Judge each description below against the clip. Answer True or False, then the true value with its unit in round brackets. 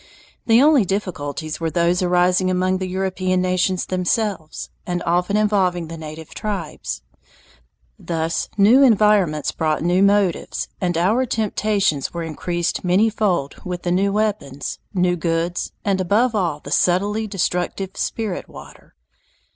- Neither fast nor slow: False (130 wpm)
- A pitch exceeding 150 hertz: True (185 Hz)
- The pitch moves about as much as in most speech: True (3.0 semitones)